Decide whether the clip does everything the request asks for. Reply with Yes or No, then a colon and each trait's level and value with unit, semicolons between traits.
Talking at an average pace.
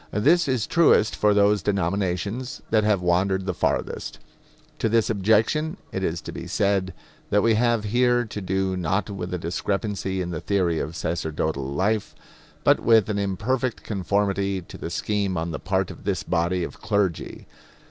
Yes: average, 170 wpm